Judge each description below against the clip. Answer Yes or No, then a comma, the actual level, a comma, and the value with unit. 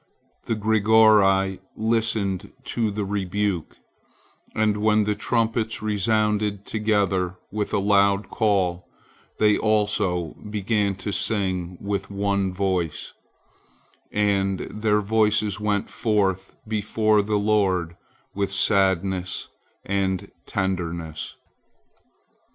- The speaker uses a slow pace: Yes, slow, 95 wpm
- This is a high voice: No, low, 100 Hz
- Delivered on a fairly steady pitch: Yes, narrow, 1.9 semitones